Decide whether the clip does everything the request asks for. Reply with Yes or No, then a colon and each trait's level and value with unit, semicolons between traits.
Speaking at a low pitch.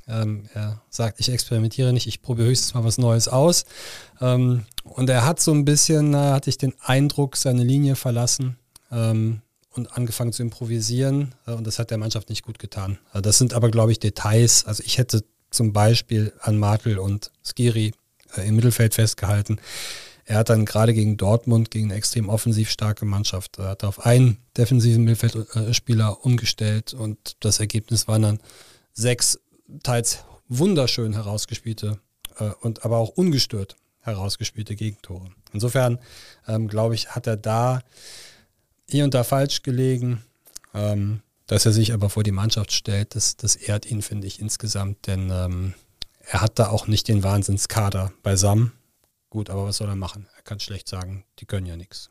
Yes: low, 110 Hz